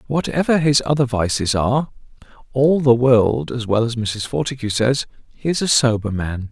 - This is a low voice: Yes, low, 125 Hz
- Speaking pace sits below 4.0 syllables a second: No, 4.9 syllables/s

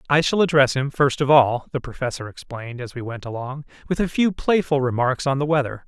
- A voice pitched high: No, low, 135 Hz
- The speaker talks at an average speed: No, fast, 225 wpm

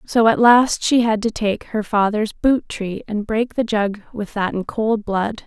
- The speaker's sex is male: No, female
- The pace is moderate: No, fast, 220 wpm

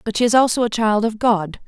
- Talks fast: Yes, fast, 285 wpm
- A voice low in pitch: No, high, 220 Hz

